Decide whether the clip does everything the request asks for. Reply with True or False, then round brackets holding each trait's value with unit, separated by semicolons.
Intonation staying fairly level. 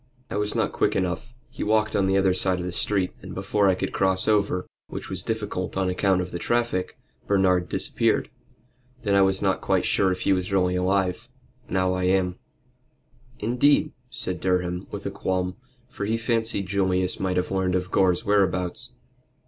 True (1.8 semitones)